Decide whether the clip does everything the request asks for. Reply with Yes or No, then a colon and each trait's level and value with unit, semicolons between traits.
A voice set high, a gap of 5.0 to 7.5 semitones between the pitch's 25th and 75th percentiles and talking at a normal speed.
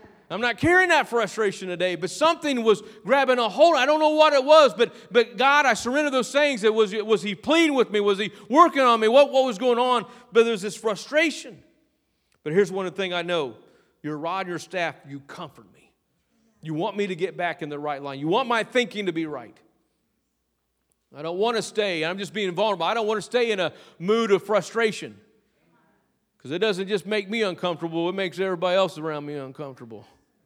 No: high, 210 Hz; wide, 5.5 semitones; fast, 215 wpm